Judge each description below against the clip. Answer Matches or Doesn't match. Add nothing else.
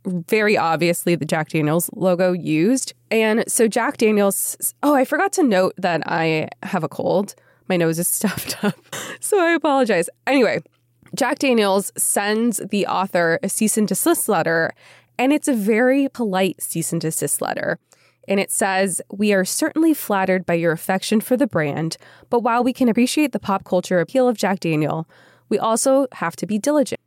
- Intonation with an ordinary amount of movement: Doesn't match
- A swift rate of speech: Doesn't match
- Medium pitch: Doesn't match